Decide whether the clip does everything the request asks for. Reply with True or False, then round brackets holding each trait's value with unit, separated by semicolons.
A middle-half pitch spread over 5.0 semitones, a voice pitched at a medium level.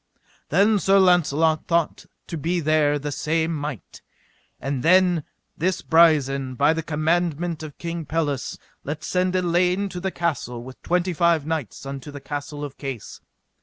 False (3.2 semitones; 160 Hz)